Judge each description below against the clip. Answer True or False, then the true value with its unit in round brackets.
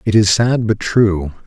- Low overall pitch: True (105 Hz)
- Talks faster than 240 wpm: False (205 wpm)